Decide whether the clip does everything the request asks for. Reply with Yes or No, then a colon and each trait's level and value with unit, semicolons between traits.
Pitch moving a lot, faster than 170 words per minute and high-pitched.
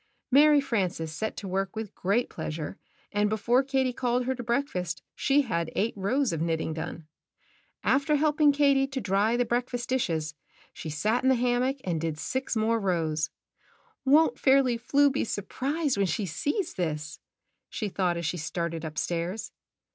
Yes: wide, 7.5 semitones; average, 180 wpm; high, 220 Hz